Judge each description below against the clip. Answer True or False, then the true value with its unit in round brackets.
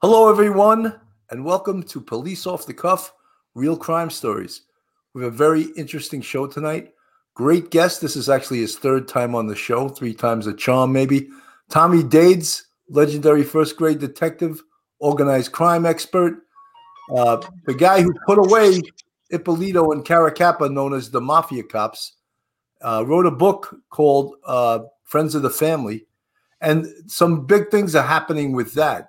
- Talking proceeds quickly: False (155 wpm)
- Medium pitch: True (155 Hz)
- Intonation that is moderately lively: True (4.6 semitones)